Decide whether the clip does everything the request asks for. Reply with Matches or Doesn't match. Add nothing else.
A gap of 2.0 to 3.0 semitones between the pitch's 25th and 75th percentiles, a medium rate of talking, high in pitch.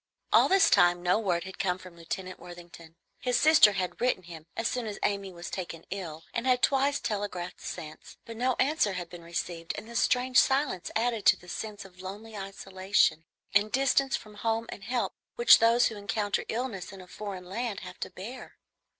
Doesn't match